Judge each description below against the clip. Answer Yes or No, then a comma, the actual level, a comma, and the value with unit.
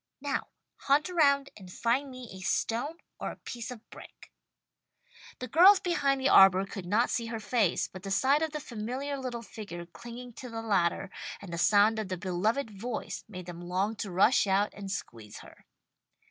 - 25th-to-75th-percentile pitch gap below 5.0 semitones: No, average, 5.3 semitones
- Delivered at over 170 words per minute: Yes, average, 190 wpm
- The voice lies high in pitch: Yes, high, 225 Hz